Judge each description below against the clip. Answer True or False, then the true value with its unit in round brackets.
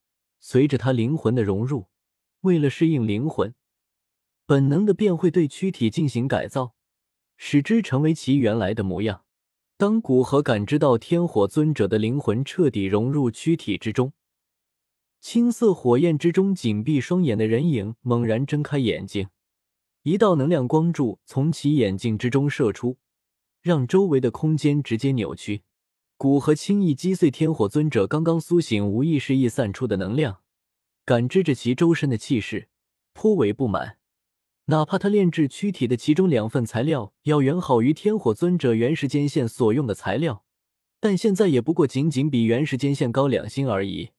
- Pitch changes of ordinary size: False (5.8 semitones)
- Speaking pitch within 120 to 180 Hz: True (135 Hz)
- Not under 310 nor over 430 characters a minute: False (250 characters per minute)